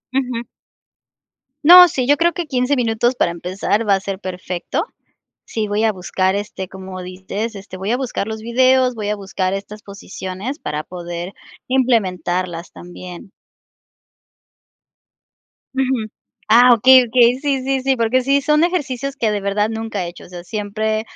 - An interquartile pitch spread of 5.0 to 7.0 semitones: Yes, average, 5.3 semitones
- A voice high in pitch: Yes, high, 220 Hz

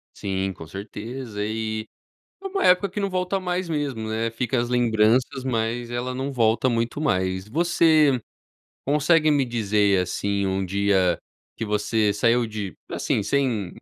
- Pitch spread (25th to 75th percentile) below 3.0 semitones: No, average, 5.2 semitones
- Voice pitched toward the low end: Yes, low, 115 Hz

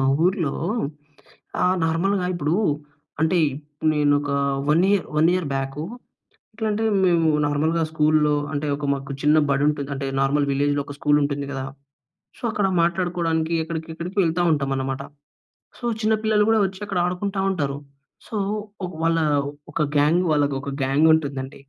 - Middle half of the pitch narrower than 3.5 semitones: No, average, 3.8 semitones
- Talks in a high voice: No, medium, 155 Hz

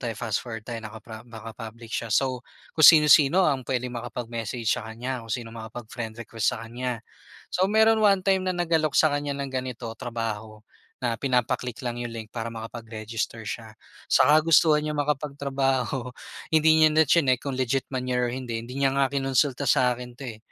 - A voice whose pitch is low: Yes, low, 125 Hz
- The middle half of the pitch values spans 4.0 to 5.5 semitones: No, average, 3.5 semitones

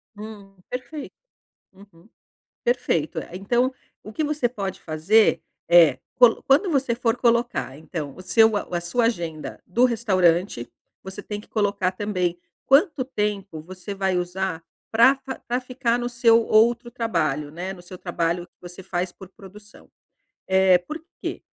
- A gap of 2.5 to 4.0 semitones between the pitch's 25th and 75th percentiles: No, average, 5.1 semitones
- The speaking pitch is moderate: No, high, 200 Hz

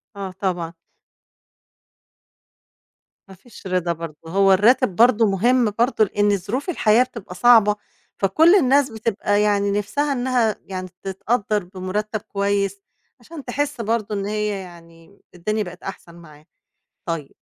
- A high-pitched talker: Yes, high, 205 Hz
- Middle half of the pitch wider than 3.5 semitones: Yes, average, 4.0 semitones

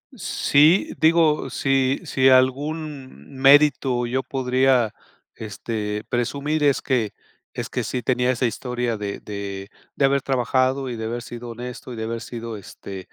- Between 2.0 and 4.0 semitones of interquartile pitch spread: Yes, average, 2.9 semitones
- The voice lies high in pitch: No, low, 130 Hz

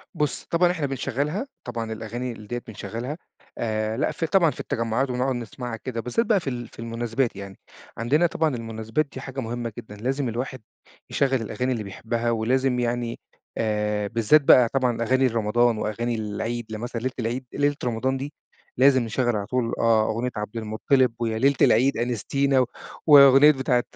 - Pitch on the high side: No, low, 120 Hz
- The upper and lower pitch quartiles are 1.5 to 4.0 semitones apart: Yes, average, 2.8 semitones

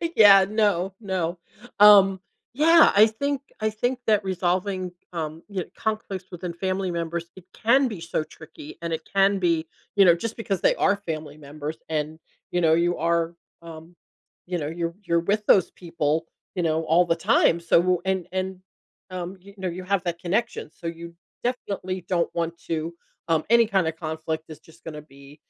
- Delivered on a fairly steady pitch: No, average, 3.1 semitones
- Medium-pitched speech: Yes, medium, 175 Hz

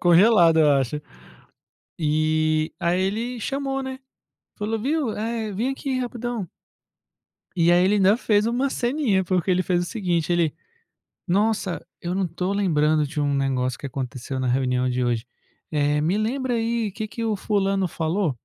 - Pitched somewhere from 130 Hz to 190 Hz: Yes, medium, 185 Hz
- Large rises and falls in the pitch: Yes, wide, 6.5 semitones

